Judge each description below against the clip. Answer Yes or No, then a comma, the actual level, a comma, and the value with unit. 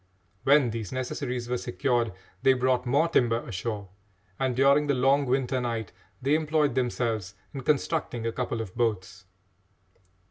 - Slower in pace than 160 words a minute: Yes, average, 145 wpm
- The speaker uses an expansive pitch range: No, average, 2.9 semitones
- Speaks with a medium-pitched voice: No, low, 125 Hz